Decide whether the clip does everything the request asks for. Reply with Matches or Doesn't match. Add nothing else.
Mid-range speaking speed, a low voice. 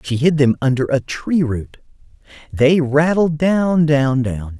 Doesn't match